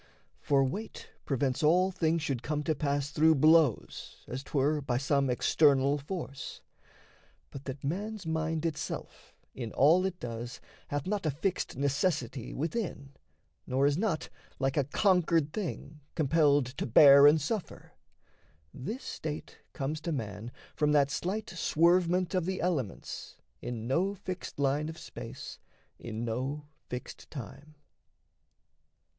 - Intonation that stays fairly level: No, average, 3.7 semitones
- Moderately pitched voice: Yes, medium, 150 Hz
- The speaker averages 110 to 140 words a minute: Yes, slow, 135 wpm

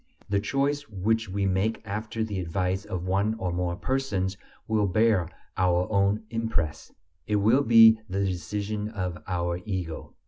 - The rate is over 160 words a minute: No, average, 150 wpm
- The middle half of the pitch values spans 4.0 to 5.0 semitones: No, average, 3.2 semitones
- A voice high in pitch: No, low, 100 Hz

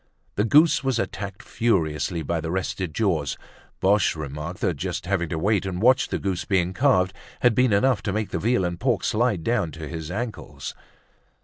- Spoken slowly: No, average, 190 wpm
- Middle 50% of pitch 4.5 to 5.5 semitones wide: Yes, average, 5.1 semitones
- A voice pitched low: Yes, very low, 95 Hz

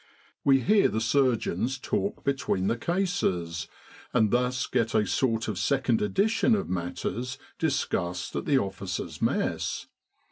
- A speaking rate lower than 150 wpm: Yes, slow, 135 wpm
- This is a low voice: Yes, low, 125 Hz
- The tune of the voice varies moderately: No, wide, 5.8 semitones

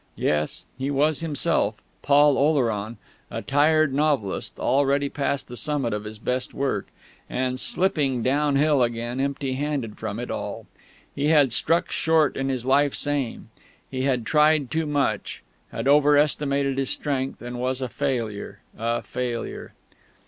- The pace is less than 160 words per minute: Yes, average, 150 wpm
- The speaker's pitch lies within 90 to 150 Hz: Yes, low, 135 Hz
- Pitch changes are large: No, average, 3.0 semitones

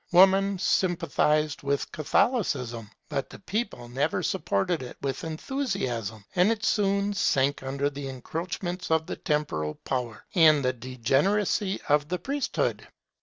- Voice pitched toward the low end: No, medium, 155 Hz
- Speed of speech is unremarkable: No, slow, 130 wpm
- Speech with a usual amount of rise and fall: No, wide, 6.4 semitones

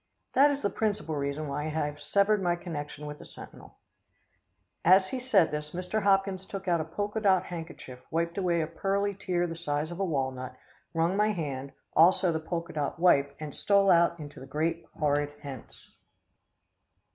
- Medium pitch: Yes, medium, 170 Hz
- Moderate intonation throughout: Yes, average, 4.5 semitones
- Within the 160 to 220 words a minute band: Yes, average, 180 wpm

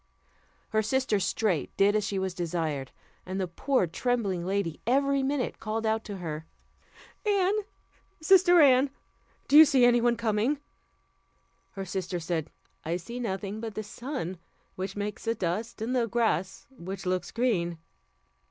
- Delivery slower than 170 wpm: Yes, average, 150 wpm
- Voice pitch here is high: Yes, high, 215 Hz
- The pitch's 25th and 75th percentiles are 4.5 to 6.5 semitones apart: Yes, average, 5.2 semitones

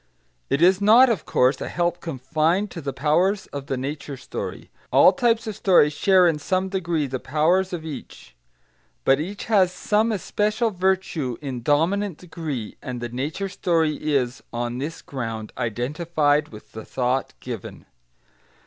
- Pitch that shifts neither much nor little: No, wide, 6.0 semitones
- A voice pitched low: No, medium, 155 Hz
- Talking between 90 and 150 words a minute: No, average, 160 wpm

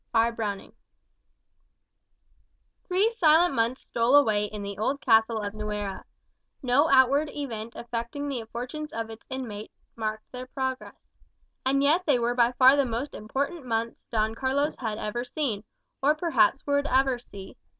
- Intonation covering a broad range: No, average, 4.1 semitones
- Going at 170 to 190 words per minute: No, average, 150 wpm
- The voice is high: Yes, high, 245 Hz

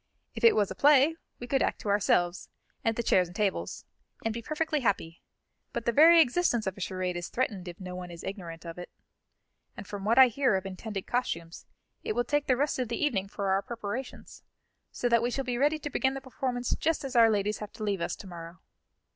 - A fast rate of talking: Yes, fast, 230 wpm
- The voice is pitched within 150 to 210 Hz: No, high, 225 Hz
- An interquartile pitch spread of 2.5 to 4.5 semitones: No, average, 5.3 semitones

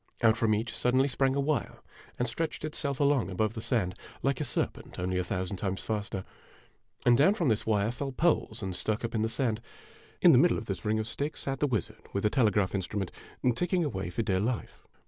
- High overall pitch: No, low, 115 Hz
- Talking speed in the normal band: No, fast, 225 wpm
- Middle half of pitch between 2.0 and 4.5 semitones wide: No, average, 5.1 semitones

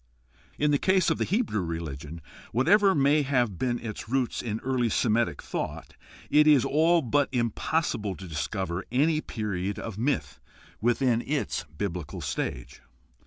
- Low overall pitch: Yes, low, 120 Hz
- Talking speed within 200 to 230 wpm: No, average, 145 wpm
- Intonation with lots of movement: Yes, wide, 6.6 semitones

